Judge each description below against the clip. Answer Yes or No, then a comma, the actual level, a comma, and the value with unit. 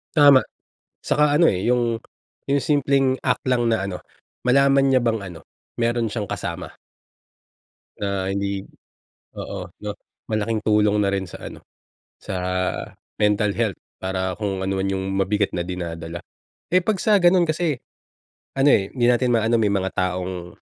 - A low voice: Yes, low, 105 Hz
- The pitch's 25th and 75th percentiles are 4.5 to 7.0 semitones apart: Yes, average, 5.3 semitones